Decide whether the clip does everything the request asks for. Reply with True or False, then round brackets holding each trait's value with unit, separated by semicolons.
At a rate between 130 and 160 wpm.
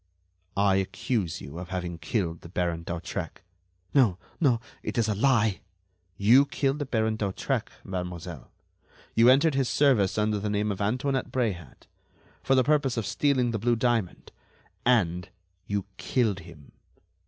True (150 wpm)